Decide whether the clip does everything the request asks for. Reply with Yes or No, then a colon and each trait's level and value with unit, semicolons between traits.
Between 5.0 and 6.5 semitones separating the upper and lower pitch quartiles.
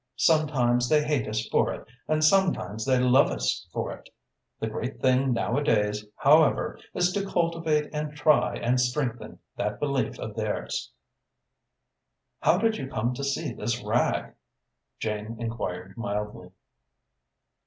Yes: average, 5.3 semitones